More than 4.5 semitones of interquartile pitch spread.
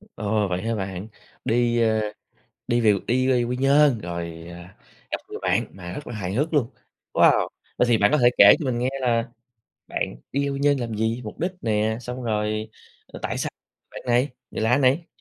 No: average, 3.3 semitones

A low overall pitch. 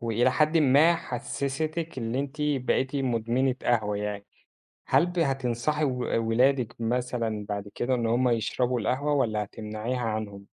Yes: low, 125 Hz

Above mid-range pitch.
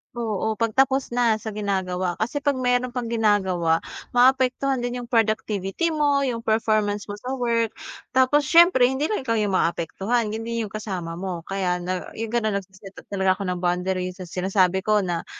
Yes: high, 215 Hz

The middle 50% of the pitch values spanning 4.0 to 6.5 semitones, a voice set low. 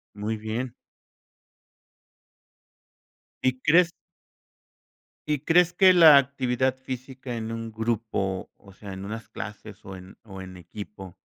Yes: average, 4.6 semitones; low, 115 Hz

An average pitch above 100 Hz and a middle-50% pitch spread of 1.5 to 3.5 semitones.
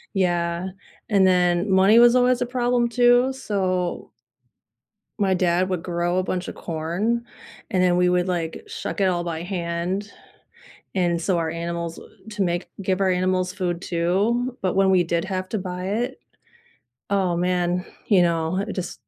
Yes: medium, 185 Hz; narrow, 2.4 semitones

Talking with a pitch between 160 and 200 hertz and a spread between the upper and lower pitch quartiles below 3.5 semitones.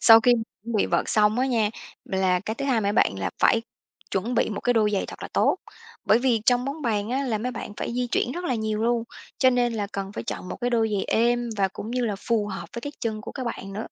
No: high, 225 Hz; average, 2.7 semitones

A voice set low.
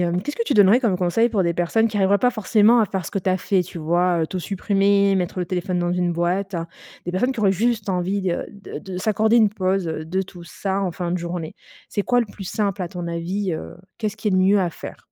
No: high, 190 Hz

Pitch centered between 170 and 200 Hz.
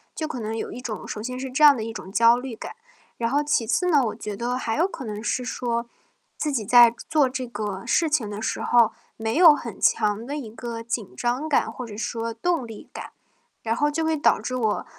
No: high, 240 Hz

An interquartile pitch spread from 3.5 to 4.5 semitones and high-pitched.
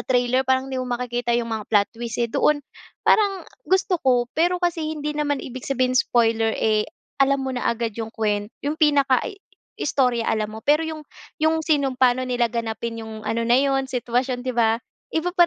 Yes: average, 4.0 semitones; very high, 255 Hz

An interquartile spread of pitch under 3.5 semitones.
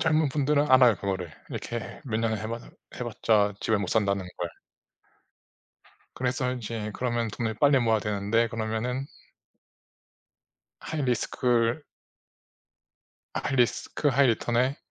Yes: average, 2.9 semitones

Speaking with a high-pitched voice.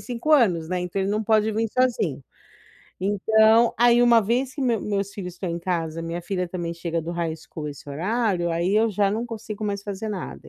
Yes: high, 200 Hz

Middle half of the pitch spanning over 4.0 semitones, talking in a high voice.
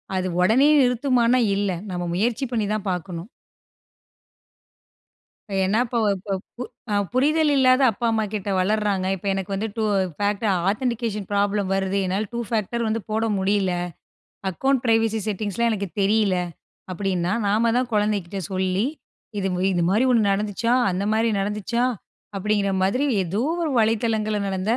No: average, 3.1 semitones; high, 210 Hz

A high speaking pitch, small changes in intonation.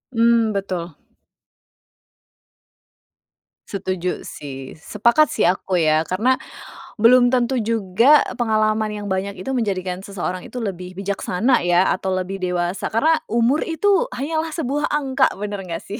No: high, 210 Hz; average, 5.2 semitones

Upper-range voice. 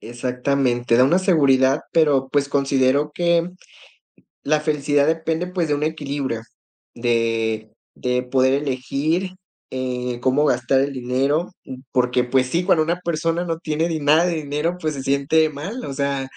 No: medium, 140 Hz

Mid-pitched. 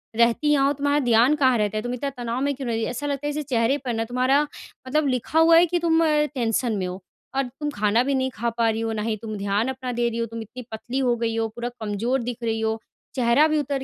No: high, 245 Hz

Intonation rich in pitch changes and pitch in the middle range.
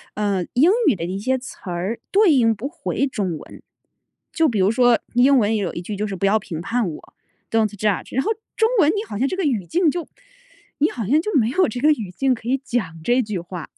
No: wide, 5.8 semitones; high, 230 Hz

